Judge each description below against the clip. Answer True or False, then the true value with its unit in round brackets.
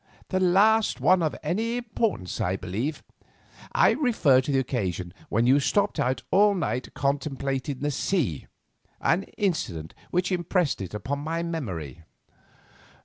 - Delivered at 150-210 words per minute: False (135 wpm)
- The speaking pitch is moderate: True (145 Hz)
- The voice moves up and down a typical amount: False (7.6 semitones)